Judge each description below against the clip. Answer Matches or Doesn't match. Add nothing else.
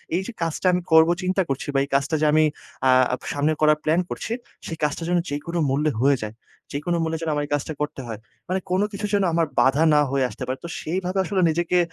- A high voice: Doesn't match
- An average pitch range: Matches